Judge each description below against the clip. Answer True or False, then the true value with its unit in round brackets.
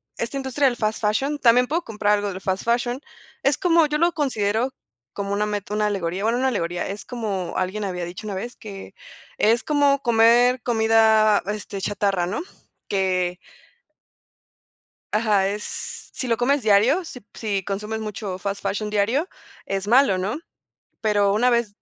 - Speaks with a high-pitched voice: True (215 Hz)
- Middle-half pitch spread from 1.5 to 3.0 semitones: False (3.5 semitones)